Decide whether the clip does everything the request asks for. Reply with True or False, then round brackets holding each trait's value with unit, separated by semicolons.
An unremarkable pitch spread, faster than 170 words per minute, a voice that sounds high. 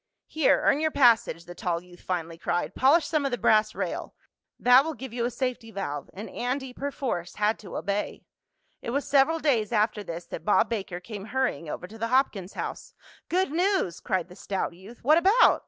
False (6.5 semitones; 200 wpm; 230 Hz)